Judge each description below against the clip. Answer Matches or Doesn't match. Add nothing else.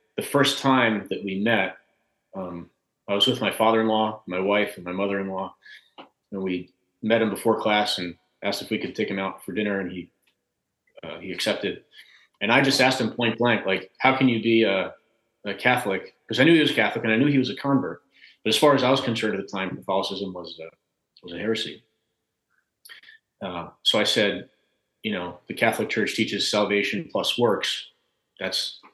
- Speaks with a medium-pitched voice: Doesn't match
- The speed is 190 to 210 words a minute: Matches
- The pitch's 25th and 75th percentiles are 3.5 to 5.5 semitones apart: Matches